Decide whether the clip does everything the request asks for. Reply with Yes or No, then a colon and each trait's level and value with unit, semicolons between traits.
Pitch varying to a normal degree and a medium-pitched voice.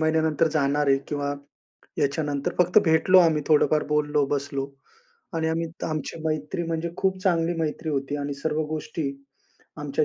No: narrow, 2.0 semitones; medium, 155 Hz